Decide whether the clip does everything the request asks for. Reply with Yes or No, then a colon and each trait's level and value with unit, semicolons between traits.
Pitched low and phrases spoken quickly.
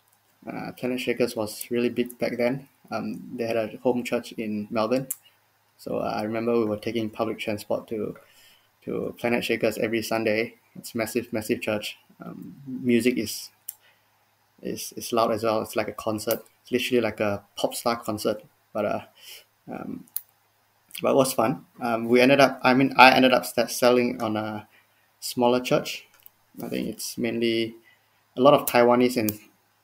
No: low, 115 Hz; average, 175 wpm